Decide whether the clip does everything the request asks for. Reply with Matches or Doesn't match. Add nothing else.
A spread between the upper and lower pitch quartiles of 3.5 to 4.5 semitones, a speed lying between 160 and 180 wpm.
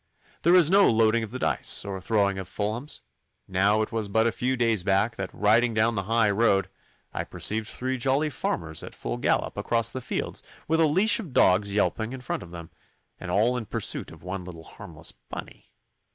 Doesn't match